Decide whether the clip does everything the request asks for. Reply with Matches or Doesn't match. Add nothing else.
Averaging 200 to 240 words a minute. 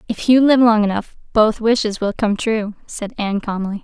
Matches